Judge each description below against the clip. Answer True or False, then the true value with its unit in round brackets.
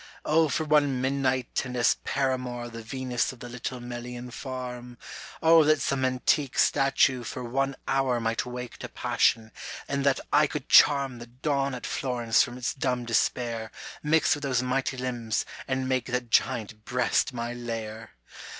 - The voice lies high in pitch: False (125 Hz)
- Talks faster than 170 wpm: False (165 wpm)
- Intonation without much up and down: True (2.0 semitones)